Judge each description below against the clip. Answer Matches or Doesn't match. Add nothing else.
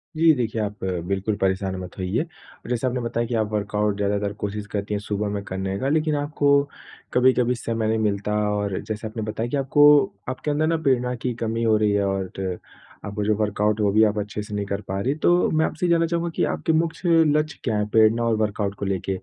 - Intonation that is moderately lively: Matches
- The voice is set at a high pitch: Doesn't match